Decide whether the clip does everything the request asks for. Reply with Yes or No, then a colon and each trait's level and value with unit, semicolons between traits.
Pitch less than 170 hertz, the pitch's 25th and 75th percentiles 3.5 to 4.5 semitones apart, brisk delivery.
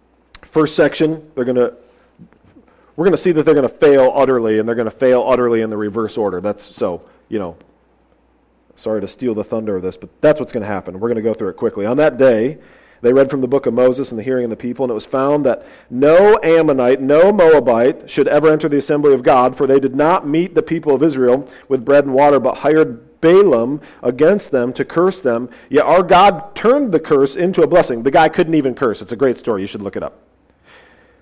Yes: low, 135 Hz; average, 3.8 semitones; fast, 240 wpm